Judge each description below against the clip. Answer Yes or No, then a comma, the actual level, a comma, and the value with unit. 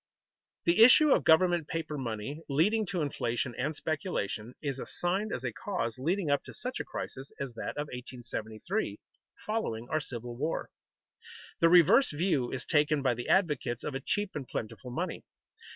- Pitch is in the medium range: Yes, medium, 150 Hz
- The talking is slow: No, average, 170 wpm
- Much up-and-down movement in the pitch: Yes, wide, 6.3 semitones